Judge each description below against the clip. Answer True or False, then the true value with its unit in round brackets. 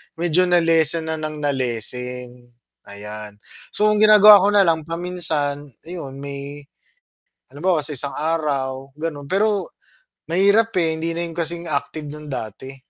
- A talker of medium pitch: True (155 Hz)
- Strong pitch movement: False (3.8 semitones)